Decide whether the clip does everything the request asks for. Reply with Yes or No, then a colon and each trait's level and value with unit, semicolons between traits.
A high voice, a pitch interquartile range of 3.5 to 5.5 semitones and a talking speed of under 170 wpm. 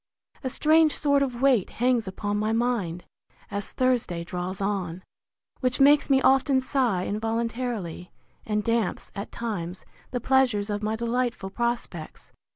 Yes: high, 230 Hz; average, 4.3 semitones; average, 140 wpm